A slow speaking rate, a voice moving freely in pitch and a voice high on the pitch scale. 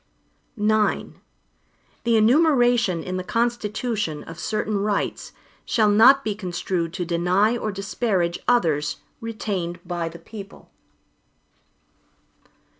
No: slow, 105 wpm; average, 4.5 semitones; high, 205 Hz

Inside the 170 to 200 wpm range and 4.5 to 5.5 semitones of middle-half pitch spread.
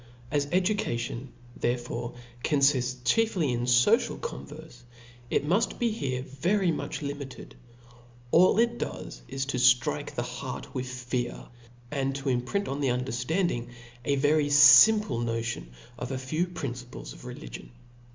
No: slow, 135 wpm; average, 4.8 semitones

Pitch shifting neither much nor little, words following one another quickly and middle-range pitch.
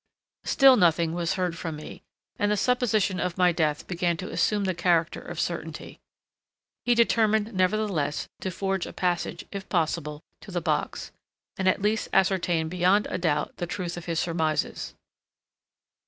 No: average, 3.2 semitones; average, 160 wpm; medium, 180 Hz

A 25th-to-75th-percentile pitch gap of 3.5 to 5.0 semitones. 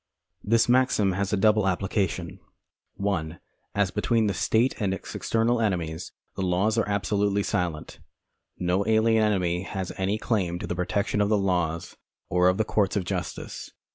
No: average, 3.0 semitones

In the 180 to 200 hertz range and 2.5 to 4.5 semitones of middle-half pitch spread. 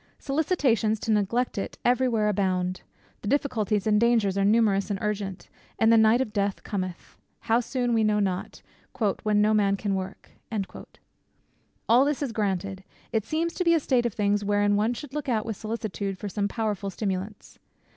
No: high, 210 Hz; average, 2.8 semitones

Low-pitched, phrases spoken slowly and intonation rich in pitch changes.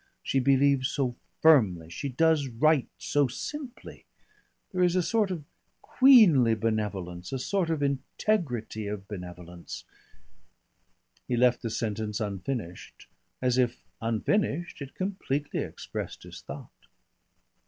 Yes: low, 130 Hz; slow, 120 wpm; wide, 6.8 semitones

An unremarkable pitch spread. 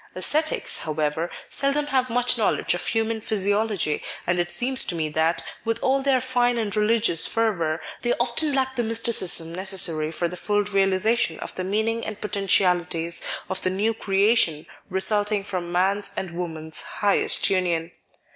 Yes: average, 4.7 semitones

